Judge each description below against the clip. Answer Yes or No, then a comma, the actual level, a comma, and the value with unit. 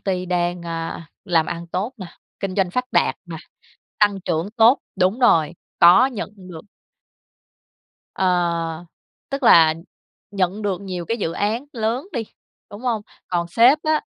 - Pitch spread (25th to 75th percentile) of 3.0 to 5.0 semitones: Yes, average, 4.5 semitones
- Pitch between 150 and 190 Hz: Yes, medium, 185 Hz